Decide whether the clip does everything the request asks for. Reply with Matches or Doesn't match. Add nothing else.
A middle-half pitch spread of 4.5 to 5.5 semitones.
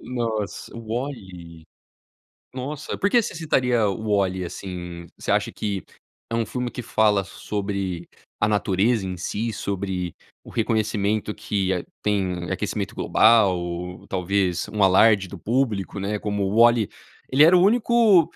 Doesn't match